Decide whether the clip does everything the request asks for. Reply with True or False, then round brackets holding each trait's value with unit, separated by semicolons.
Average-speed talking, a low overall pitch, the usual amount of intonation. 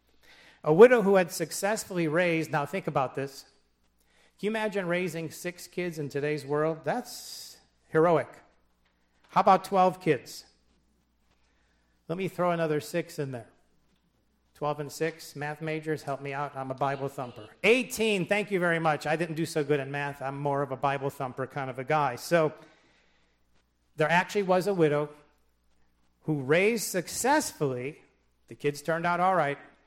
False (165 wpm; 150 Hz; 4.8 semitones)